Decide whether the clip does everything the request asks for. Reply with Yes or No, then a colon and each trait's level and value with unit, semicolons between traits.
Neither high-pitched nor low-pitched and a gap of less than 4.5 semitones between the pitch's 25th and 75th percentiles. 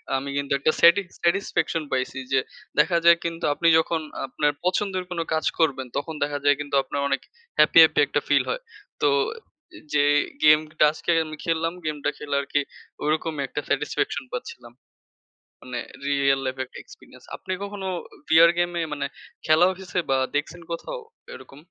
Yes: medium, 155 Hz; average, 3.1 semitones